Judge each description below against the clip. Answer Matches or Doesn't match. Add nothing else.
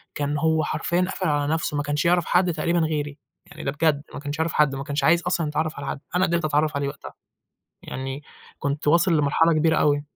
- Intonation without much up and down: Matches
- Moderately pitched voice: Matches